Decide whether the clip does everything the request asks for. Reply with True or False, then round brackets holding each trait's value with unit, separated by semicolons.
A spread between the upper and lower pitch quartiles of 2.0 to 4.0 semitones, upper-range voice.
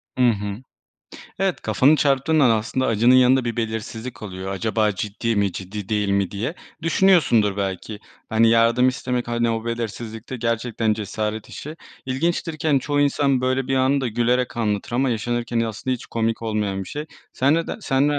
False (3.3 semitones; 115 Hz)